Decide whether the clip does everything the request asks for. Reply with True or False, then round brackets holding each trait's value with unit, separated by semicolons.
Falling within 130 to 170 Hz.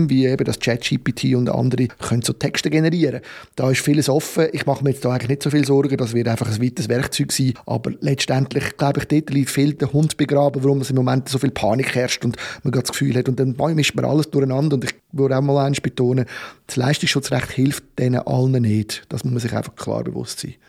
True (135 Hz)